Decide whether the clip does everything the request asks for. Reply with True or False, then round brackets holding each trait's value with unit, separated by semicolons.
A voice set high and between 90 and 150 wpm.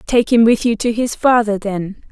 False (225 Hz; 225 wpm)